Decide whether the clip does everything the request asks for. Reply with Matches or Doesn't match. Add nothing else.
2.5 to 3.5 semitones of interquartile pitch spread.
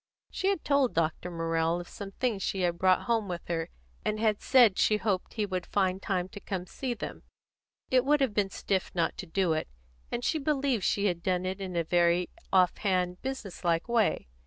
Doesn't match